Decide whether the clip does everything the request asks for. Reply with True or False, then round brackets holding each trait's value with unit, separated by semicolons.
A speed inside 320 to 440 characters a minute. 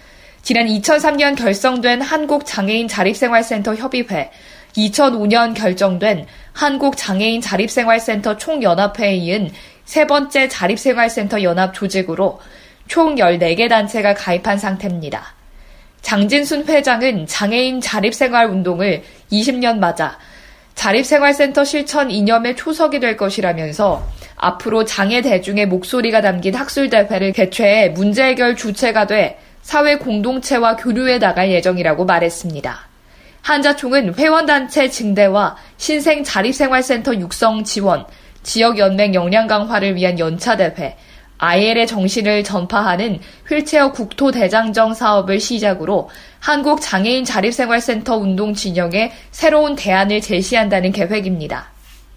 False (295 characters per minute)